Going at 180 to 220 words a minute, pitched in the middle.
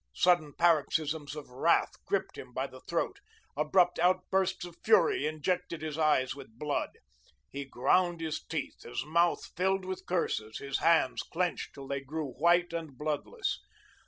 No: average, 155 wpm; medium, 160 Hz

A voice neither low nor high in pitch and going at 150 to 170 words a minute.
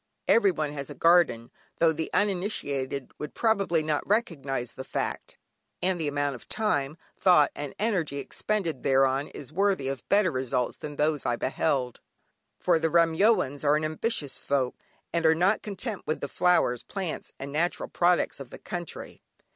Yes: medium, 155 Hz; average, 160 wpm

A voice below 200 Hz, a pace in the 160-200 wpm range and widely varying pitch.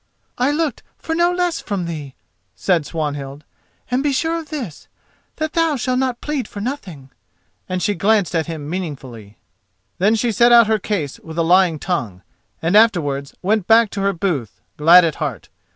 Yes: high, 190 Hz; average, 180 wpm; wide, 7.7 semitones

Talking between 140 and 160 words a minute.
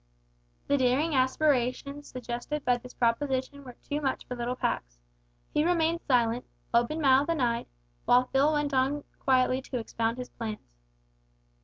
Yes: average, 150 wpm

